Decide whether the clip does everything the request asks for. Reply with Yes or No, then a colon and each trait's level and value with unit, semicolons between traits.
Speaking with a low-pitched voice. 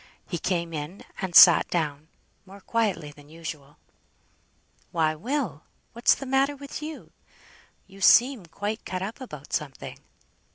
No: medium, 185 Hz